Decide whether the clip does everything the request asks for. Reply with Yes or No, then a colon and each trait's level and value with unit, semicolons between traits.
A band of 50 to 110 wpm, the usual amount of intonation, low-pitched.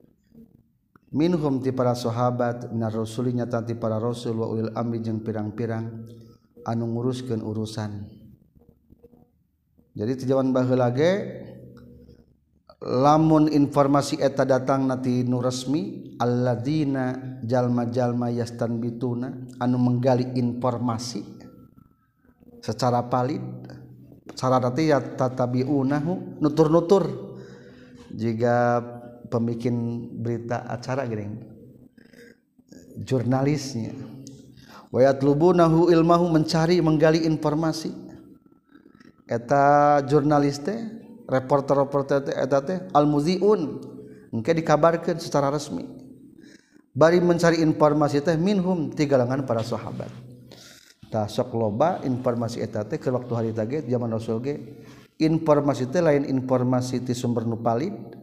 Yes: average, 90 wpm; average, 4.0 semitones; low, 125 Hz